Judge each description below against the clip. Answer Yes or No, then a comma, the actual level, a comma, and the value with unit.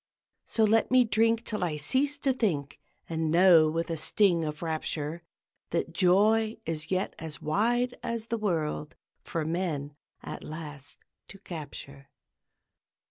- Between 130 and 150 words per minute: Yes, average, 140 wpm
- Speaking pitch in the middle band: Yes, medium, 170 Hz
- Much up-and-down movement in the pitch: Yes, wide, 6.0 semitones